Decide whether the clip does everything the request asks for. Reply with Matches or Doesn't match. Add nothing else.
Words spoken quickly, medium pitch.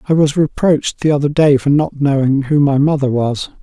Matches